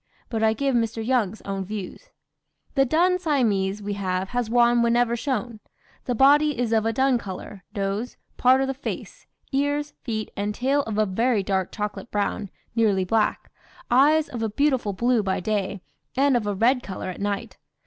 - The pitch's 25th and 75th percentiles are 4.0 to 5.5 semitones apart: Yes, average, 4.4 semitones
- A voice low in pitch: No, high, 225 Hz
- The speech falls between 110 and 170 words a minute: No, average, 180 wpm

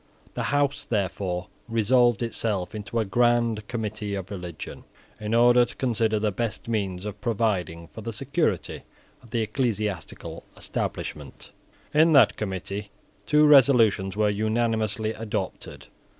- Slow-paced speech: Yes, slow, 130 wpm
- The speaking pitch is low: Yes, low, 110 Hz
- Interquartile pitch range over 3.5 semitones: No, average, 3.1 semitones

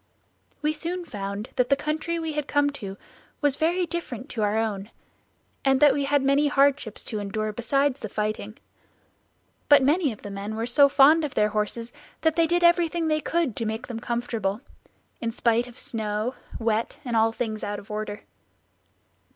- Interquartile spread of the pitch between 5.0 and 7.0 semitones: Yes, wide, 5.4 semitones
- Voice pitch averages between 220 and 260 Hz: Yes, high, 245 Hz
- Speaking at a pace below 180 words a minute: No, average, 185 wpm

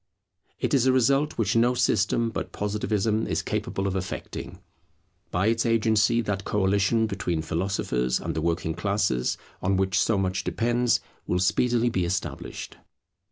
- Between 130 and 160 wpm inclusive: Yes, average, 150 wpm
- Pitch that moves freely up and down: No, average, 3.5 semitones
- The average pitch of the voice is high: No, low, 105 Hz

